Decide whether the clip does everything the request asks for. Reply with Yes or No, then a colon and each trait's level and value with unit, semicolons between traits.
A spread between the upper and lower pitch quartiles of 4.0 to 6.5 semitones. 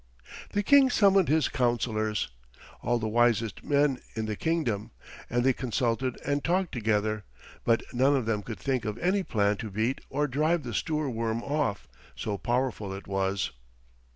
Yes: average, 5.1 semitones